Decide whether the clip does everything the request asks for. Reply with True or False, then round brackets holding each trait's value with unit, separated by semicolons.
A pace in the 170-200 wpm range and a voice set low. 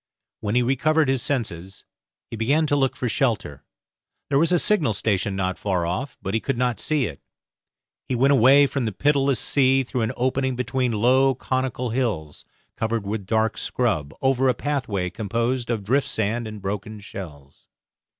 True (175 wpm; 120 Hz)